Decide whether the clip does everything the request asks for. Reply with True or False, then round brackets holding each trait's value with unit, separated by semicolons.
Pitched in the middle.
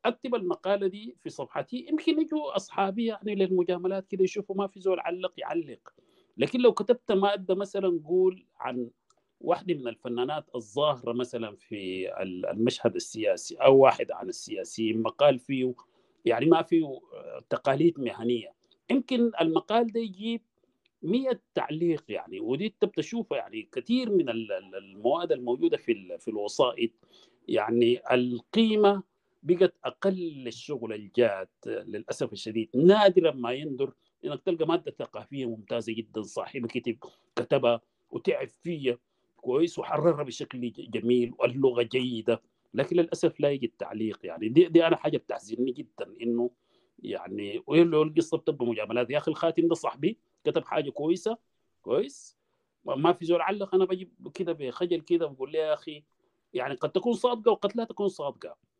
True (170 Hz)